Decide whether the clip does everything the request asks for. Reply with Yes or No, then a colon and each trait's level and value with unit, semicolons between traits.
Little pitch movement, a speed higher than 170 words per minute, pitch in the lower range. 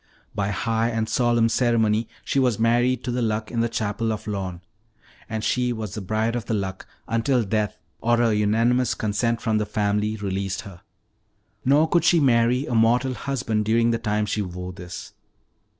Yes: narrow, 2.2 semitones; average, 180 wpm; low, 115 Hz